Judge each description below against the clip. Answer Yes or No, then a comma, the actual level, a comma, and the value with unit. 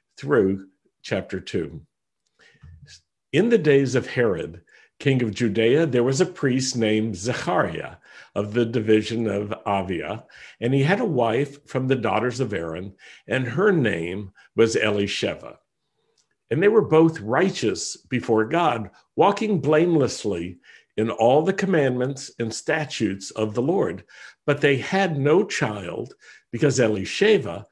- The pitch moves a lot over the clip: Yes, wide, 5.7 semitones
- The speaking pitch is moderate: No, low, 125 Hz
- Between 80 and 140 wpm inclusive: Yes, slow, 135 wpm